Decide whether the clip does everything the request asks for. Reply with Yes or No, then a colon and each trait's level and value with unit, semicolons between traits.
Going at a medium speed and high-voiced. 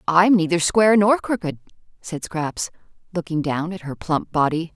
No: average, 175 wpm; medium, 175 Hz